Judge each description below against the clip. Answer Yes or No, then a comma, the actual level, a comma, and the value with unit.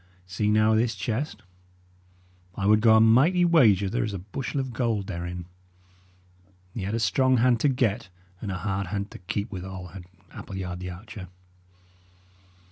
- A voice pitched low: Yes, low, 105 Hz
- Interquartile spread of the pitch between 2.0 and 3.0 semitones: No, average, 3.7 semitones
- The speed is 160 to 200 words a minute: Yes, average, 165 wpm